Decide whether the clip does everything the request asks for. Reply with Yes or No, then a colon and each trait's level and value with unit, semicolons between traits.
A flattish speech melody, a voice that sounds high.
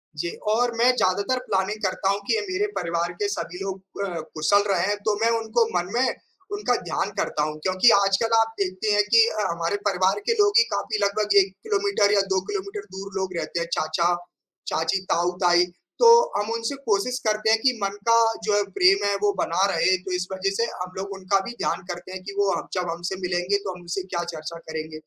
No: average, 3.3 semitones; high, 195 Hz